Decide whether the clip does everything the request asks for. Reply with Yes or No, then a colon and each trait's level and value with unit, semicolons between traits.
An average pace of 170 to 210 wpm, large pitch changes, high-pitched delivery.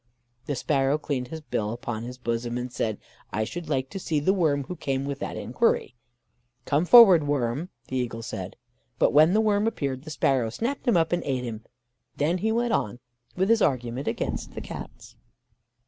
No: average, 195 wpm; wide, 6.1 semitones; medium, 140 Hz